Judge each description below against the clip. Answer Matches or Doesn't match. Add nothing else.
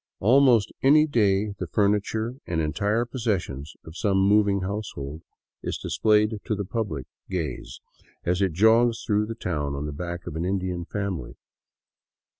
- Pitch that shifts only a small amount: Doesn't match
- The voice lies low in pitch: Matches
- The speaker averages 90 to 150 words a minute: Matches